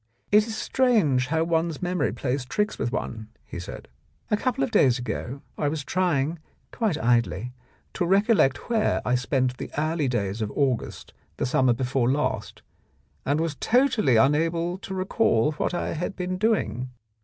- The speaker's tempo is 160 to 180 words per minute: Yes, average, 170 wpm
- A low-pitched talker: No, medium, 150 Hz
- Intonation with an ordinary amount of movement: No, wide, 6.4 semitones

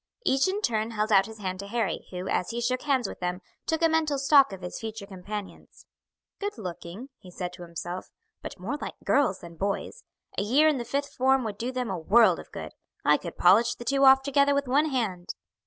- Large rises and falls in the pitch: Yes, wide, 6.1 semitones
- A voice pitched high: Yes, high, 230 Hz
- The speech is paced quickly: Yes, fast, 225 wpm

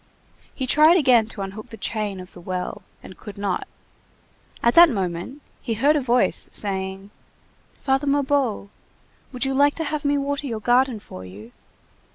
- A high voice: Yes, high, 235 Hz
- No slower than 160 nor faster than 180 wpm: Yes, average, 170 wpm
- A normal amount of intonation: No, wide, 6.2 semitones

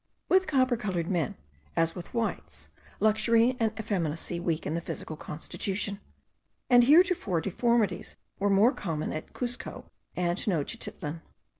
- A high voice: Yes, high, 200 Hz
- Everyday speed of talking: No, slow, 125 wpm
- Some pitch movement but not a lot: No, wide, 5.8 semitones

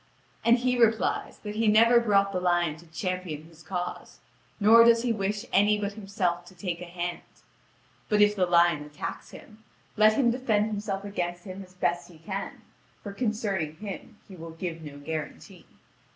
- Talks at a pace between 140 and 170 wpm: No, average, 180 wpm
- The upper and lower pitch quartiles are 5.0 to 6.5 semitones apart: No, average, 3.5 semitones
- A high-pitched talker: Yes, high, 195 Hz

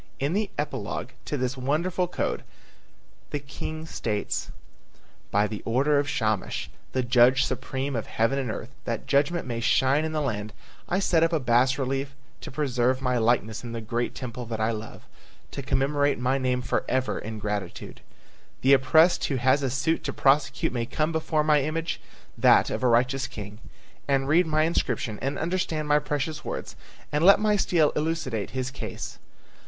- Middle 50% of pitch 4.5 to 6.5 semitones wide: No, average, 4.0 semitones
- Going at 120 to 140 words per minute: No, average, 175 wpm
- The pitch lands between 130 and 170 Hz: Yes, low, 135 Hz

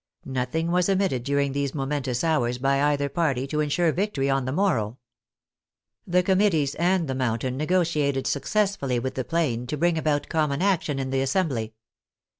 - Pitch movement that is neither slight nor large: Yes, average, 4.2 semitones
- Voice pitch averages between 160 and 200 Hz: No, medium, 140 Hz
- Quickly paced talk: No, average, 165 wpm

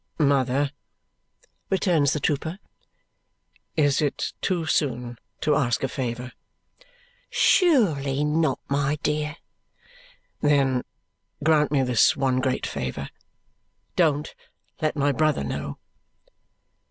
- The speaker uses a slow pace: Yes, slow, 100 wpm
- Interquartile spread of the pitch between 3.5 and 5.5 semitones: No, average, 2.8 semitones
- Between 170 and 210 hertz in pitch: No, medium, 145 Hz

